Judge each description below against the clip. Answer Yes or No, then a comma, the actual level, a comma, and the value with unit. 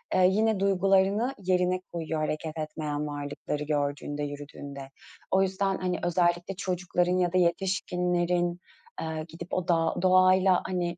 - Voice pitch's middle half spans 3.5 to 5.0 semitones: No, average, 2.9 semitones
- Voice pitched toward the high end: No, medium, 175 Hz